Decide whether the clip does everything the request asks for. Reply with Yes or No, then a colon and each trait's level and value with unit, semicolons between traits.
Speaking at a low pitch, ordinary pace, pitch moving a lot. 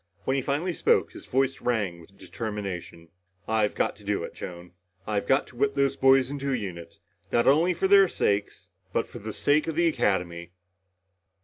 Yes: low, 120 Hz; average, 190 wpm; wide, 6.2 semitones